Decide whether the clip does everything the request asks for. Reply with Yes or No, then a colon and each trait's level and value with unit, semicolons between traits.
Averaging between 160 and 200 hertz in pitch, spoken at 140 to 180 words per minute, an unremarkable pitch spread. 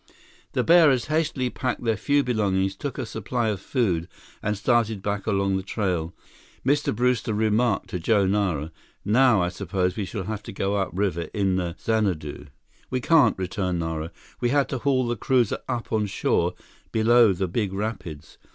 No: low, 105 Hz; average, 170 wpm; average, 4.2 semitones